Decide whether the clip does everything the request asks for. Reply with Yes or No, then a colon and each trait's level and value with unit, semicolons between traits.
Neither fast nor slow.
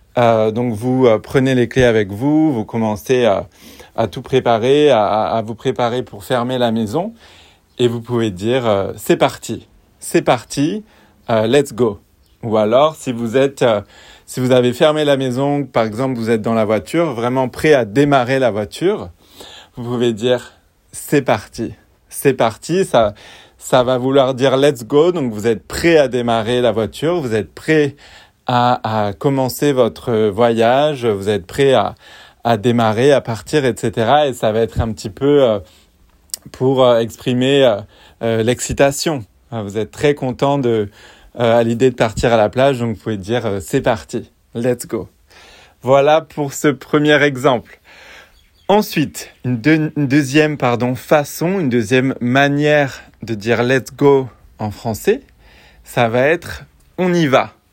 Yes: average, 160 wpm